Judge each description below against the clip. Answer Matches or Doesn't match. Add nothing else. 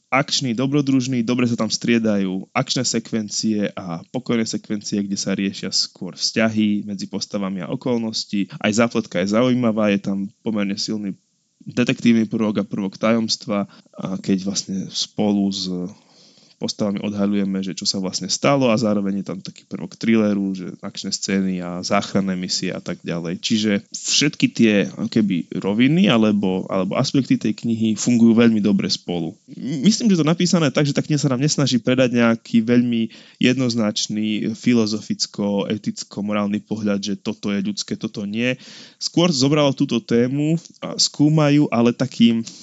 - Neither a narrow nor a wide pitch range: Matches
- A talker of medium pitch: Doesn't match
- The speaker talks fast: Doesn't match